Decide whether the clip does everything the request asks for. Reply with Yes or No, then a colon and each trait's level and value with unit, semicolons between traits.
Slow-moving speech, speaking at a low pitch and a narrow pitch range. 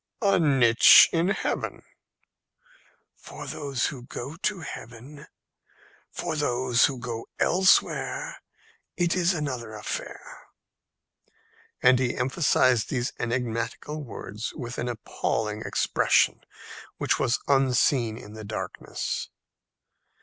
No: slow, 105 wpm; low, 125 Hz; average, 4.2 semitones